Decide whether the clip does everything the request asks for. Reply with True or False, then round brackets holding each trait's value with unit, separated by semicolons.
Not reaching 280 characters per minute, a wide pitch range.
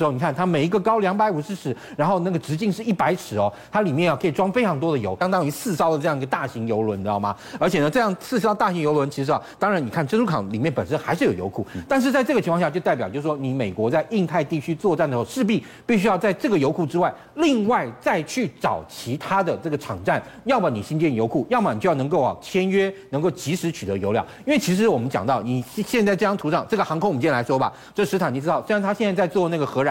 False (405 characters per minute; 6.4 semitones)